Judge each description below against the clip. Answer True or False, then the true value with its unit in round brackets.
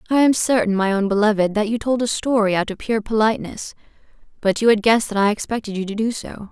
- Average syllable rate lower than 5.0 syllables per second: False (6.4 syllables/s)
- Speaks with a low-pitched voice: False (215 Hz)